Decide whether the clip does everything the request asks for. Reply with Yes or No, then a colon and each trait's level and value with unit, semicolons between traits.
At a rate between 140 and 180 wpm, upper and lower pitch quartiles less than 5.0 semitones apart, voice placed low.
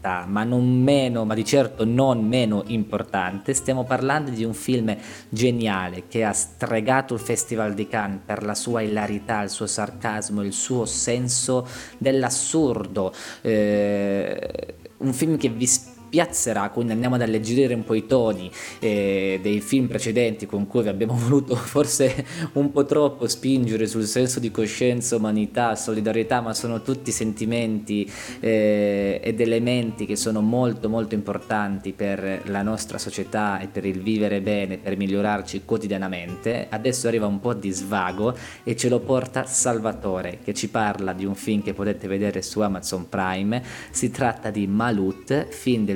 Yes: average, 155 wpm; average, 3.3 semitones; low, 110 Hz